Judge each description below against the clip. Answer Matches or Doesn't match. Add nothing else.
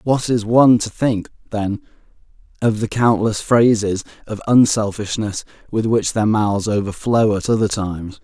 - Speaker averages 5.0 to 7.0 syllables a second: Doesn't match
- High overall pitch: Doesn't match